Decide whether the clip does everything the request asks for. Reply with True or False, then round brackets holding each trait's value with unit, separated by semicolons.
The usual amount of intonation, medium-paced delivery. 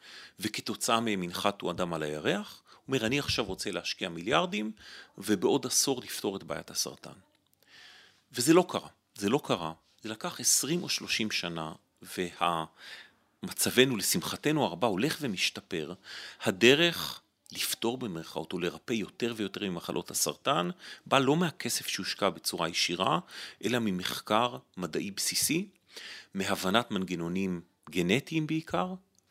False (5.8 semitones; 120 wpm)